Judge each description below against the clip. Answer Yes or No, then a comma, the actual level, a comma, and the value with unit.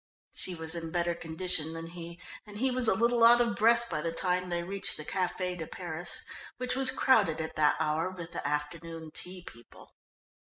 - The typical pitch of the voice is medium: Yes, medium, 175 Hz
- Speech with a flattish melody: No, average, 4.3 semitones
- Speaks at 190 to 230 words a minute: Yes, average, 200 wpm